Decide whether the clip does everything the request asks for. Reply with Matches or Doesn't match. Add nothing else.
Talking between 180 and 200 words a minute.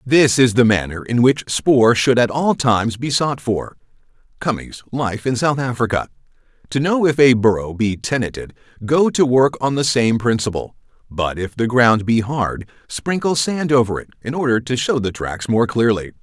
Matches